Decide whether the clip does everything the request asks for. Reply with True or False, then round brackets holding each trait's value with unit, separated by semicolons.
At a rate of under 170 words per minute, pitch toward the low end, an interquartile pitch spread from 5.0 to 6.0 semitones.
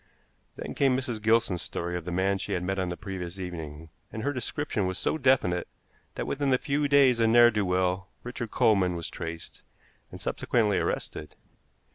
False (185 wpm; 100 Hz; 5.3 semitones)